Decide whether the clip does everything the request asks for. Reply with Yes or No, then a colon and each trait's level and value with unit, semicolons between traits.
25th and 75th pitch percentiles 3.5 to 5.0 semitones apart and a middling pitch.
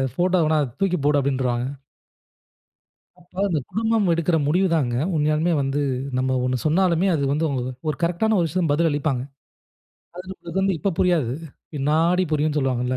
Yes: average, 4.3 semitones; medium, 155 Hz